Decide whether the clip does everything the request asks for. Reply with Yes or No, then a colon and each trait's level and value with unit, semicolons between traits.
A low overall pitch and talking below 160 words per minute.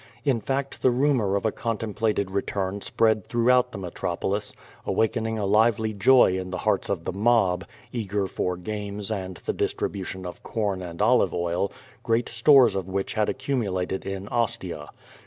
No: low, 105 Hz; average, 175 wpm